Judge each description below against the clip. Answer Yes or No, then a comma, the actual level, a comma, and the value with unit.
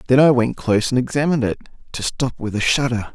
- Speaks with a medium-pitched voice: No, low, 125 Hz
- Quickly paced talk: Yes, fast, 230 wpm